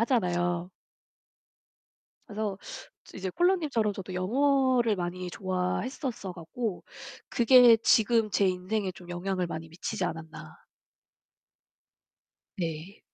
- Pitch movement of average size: Yes, average, 4.6 semitones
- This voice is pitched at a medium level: No, high, 195 Hz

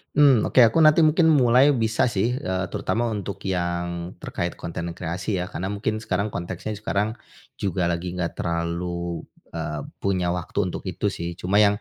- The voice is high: No, very low, 95 Hz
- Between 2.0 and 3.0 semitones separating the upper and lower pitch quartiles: No, average, 3.7 semitones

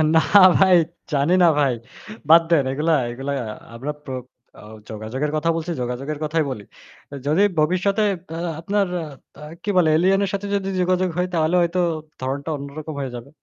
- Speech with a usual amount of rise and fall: Yes, average, 4.4 semitones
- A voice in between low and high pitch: Yes, medium, 155 Hz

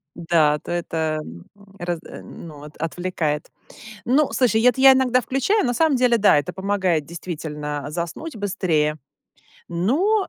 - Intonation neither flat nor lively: No, wide, 8.1 semitones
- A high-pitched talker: No, medium, 175 Hz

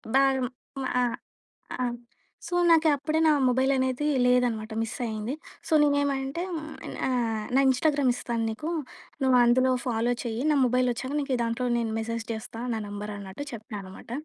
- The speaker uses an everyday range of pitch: Yes, average, 3.0 semitones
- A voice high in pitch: Yes, very high, 250 Hz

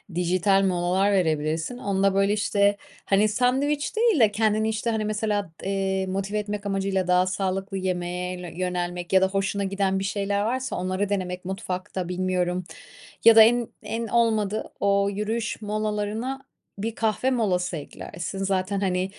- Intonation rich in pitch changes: No, narrow, 2.5 semitones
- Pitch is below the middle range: No, high, 195 Hz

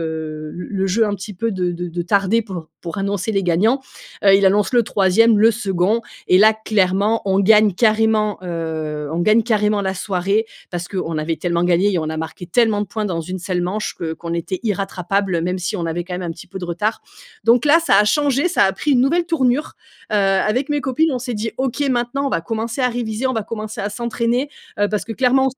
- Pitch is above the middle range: Yes, high, 205 Hz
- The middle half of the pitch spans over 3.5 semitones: Yes, average, 4.3 semitones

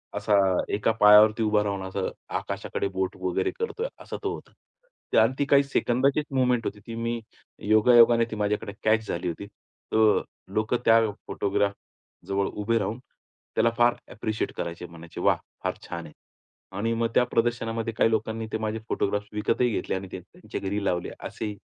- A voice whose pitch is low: Yes, low, 110 Hz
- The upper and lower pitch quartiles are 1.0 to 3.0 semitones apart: Yes, narrow, 2.4 semitones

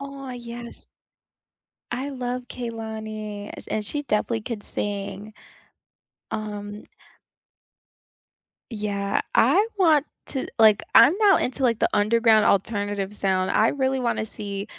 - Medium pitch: No, high, 220 Hz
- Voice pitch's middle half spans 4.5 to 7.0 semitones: No, average, 3.4 semitones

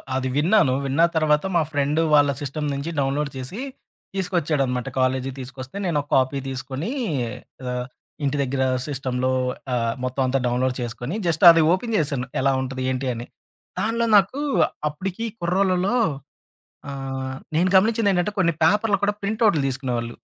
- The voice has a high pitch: No, medium, 140 Hz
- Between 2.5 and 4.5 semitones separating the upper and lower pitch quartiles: No, wide, 5.4 semitones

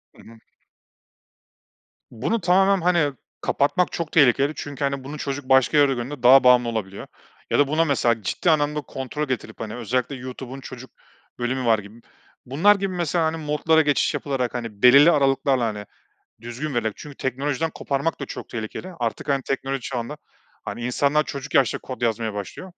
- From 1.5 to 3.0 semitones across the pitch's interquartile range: No, average, 3.6 semitones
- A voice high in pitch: No, low, 135 Hz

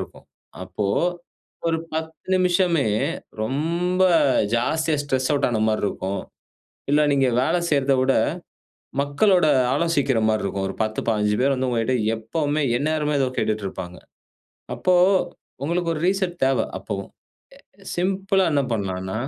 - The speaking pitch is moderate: Yes, medium, 145 Hz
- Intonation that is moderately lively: No, wide, 7.0 semitones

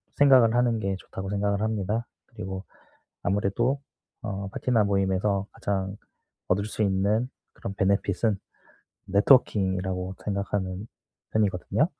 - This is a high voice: No, low, 100 Hz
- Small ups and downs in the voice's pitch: Yes, narrow, 2.3 semitones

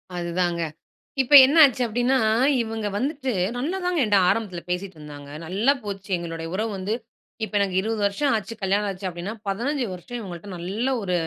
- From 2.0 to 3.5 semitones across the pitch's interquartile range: No, average, 5.1 semitones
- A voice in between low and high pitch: No, high, 200 Hz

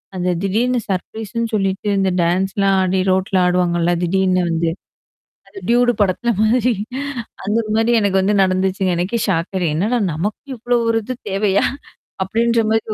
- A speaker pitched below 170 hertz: No, high, 195 Hz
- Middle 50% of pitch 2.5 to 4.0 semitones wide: Yes, average, 3.4 semitones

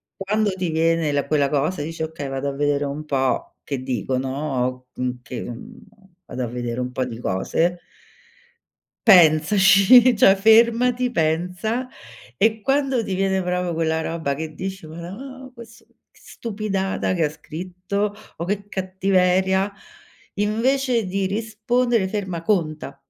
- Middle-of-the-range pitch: Yes, medium, 180 Hz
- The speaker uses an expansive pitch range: Yes, wide, 5.7 semitones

